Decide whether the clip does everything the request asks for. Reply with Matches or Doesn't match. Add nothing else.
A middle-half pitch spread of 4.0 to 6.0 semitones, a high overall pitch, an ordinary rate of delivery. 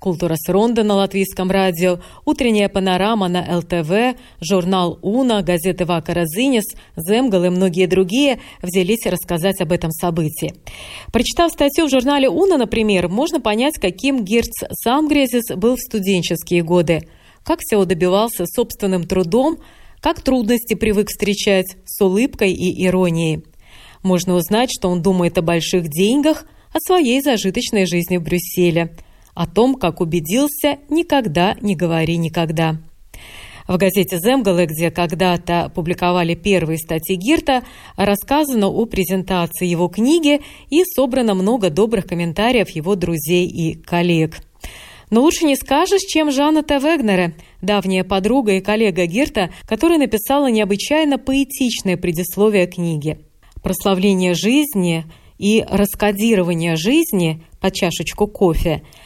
Matches